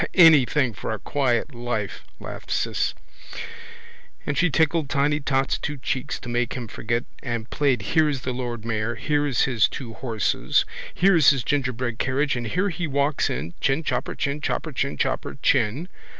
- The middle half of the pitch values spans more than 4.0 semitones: No, average, 3.7 semitones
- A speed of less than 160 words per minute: Yes, average, 150 wpm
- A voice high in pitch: No, low, 135 Hz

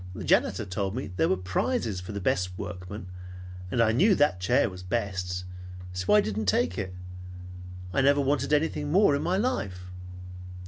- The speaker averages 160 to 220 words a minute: Yes, average, 175 wpm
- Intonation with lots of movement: Yes, wide, 7.6 semitones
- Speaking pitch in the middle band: No, low, 100 Hz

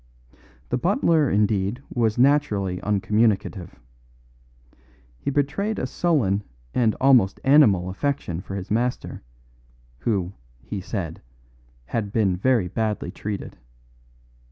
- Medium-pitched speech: No, low, 110 Hz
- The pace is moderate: No, slow, 105 wpm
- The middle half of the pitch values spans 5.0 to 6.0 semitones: Yes, wide, 5.4 semitones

